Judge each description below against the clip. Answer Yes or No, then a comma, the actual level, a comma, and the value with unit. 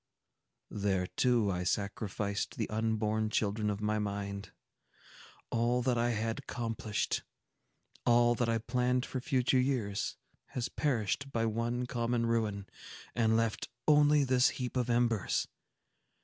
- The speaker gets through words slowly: Yes, slow, 120 wpm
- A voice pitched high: No, low, 115 Hz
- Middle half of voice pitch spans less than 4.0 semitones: Yes, average, 2.7 semitones